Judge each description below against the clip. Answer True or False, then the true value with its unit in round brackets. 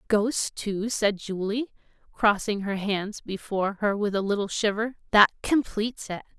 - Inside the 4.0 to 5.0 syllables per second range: True (4.6 syllables/s)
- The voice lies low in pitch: False (210 Hz)